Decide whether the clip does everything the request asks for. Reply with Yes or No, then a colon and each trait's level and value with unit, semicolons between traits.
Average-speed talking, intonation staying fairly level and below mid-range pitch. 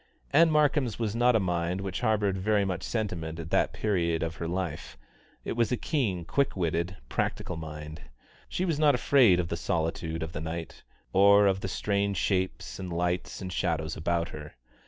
No: average, 185 wpm; average, 4.4 semitones; very low, 95 Hz